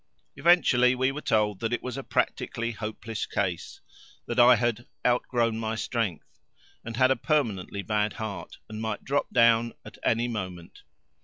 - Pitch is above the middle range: No, low, 115 Hz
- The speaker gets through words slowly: No, average, 160 wpm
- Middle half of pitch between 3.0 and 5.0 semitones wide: No, narrow, 2.4 semitones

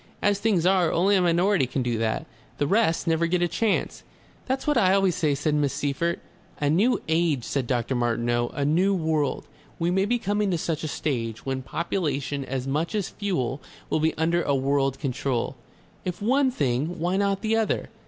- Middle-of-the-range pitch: Yes, medium, 160 Hz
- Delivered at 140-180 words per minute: No, average, 195 wpm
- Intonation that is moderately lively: No, wide, 6.0 semitones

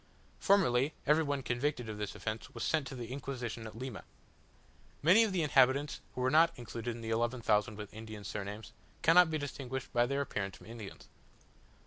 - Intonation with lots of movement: No, average, 4.4 semitones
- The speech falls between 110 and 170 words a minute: No, average, 185 wpm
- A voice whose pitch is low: Yes, low, 125 Hz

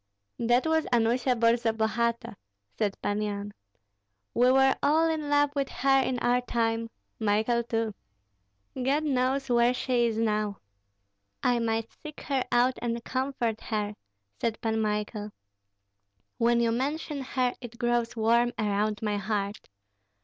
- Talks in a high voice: Yes, high, 235 Hz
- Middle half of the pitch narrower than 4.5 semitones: Yes, average, 2.7 semitones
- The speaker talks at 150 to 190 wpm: No, slow, 135 wpm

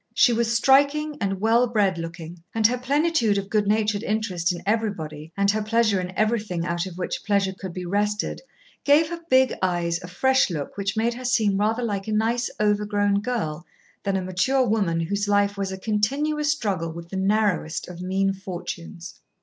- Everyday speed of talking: Yes, average, 190 wpm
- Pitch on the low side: No, high, 205 Hz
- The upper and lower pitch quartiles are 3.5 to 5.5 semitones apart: Yes, average, 3.8 semitones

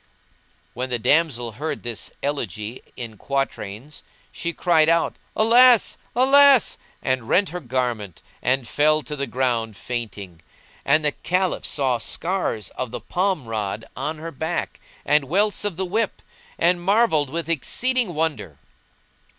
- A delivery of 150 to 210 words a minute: No, average, 140 wpm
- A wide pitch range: Yes, wide, 6.7 semitones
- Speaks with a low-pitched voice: No, medium, 150 Hz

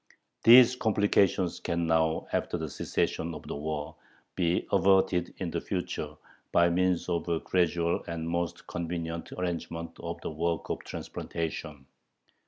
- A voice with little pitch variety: Yes, narrow, 1.6 semitones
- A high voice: No, very low, 85 Hz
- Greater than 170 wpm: No, average, 140 wpm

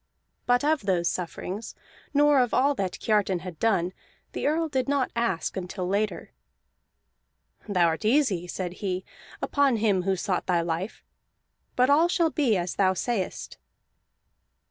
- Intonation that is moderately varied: No, wide, 6.3 semitones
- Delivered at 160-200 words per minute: No, average, 145 wpm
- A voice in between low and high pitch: No, high, 205 Hz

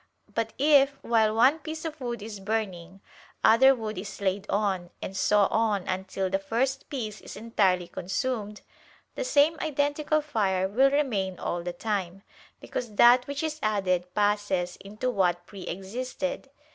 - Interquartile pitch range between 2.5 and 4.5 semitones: No, wide, 5.4 semitones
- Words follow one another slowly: No, average, 155 wpm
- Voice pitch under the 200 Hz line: No, high, 215 Hz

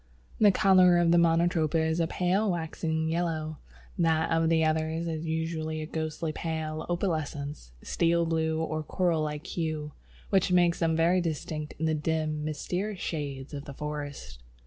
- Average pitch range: No, narrow, 1.5 semitones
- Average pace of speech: Yes, average, 155 wpm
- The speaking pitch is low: No, medium, 160 Hz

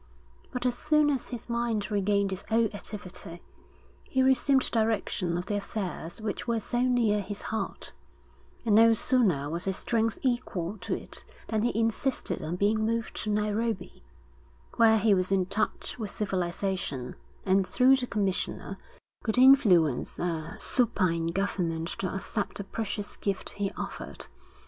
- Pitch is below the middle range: No, high, 210 Hz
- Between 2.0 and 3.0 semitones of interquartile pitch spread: No, average, 3.7 semitones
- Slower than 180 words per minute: Yes, average, 150 wpm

